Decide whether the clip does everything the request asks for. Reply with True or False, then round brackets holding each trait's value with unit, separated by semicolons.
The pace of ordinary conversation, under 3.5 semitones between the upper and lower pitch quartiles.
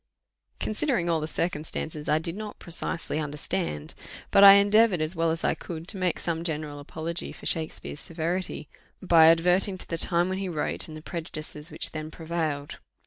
True (180 wpm; 2.5 semitones)